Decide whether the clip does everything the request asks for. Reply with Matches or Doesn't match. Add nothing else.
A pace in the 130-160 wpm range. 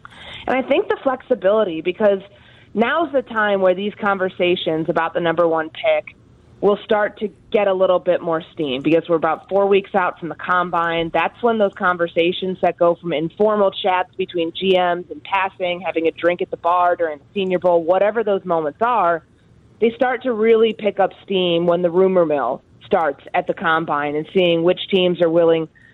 Doesn't match